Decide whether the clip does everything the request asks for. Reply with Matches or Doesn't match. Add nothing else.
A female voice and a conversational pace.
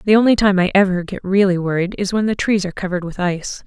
Doesn't match